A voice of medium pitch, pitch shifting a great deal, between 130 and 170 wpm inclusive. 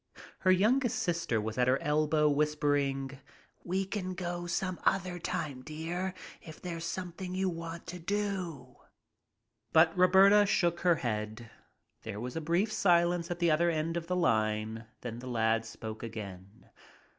Yes: medium, 165 Hz; wide, 6.1 semitones; average, 155 wpm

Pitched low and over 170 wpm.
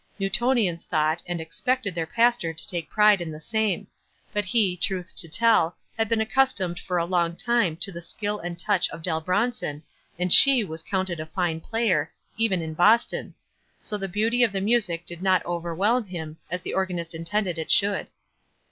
No: medium, 185 Hz; average, 190 wpm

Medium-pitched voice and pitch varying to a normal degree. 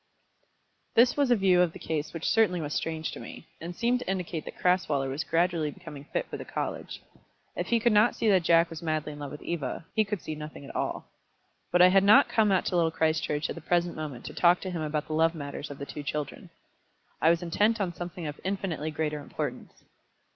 Yes: medium, 165 Hz; average, 3.6 semitones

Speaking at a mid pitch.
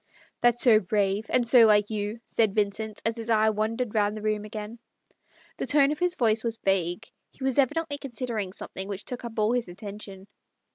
No: high, 220 Hz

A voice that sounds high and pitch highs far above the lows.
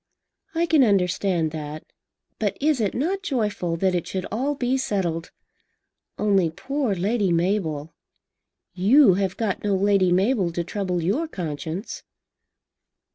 Yes: high, 195 Hz; wide, 5.7 semitones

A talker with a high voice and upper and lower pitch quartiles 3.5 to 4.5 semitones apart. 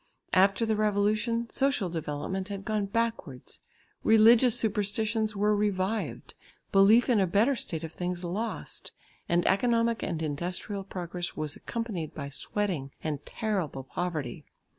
Yes: high, 200 Hz; average, 4.1 semitones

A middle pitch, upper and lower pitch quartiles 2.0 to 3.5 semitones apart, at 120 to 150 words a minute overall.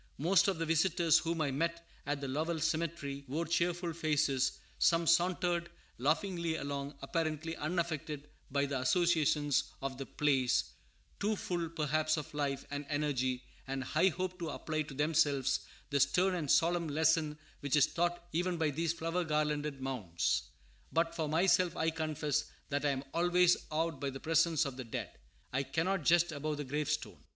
No: medium, 155 Hz; average, 3.0 semitones; average, 165 wpm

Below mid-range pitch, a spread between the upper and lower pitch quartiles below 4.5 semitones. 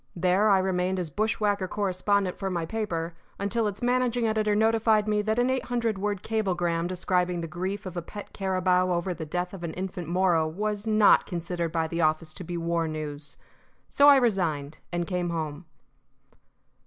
No: medium, 185 Hz; average, 3.7 semitones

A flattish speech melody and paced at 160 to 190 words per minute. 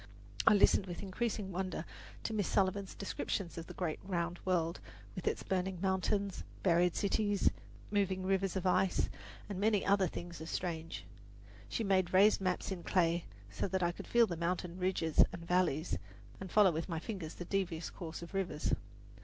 Yes: narrow, 2.3 semitones; average, 175 wpm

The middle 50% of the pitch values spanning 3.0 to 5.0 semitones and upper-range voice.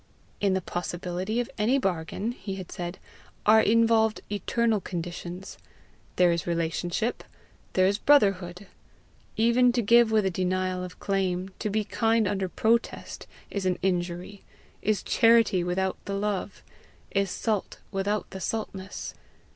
Yes: average, 3.3 semitones; high, 195 Hz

